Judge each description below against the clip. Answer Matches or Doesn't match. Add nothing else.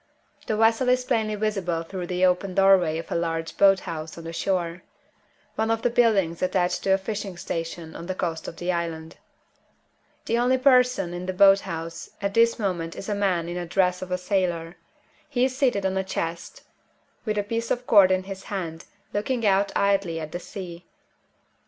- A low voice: Doesn't match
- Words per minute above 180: Matches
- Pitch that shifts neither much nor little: Matches